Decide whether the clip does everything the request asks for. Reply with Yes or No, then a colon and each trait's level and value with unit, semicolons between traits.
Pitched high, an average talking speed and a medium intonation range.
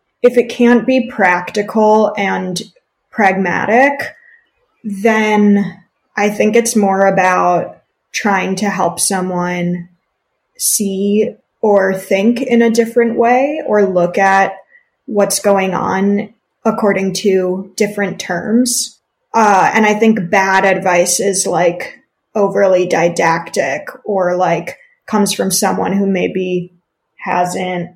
No: high, 200 Hz; slow, 110 wpm; average, 3.4 semitones